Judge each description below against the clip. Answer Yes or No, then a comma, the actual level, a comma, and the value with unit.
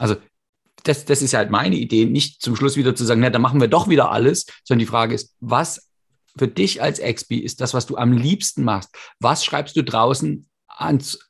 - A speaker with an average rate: No, fast, 220 wpm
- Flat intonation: No, average, 3.7 semitones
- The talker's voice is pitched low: Yes, low, 125 Hz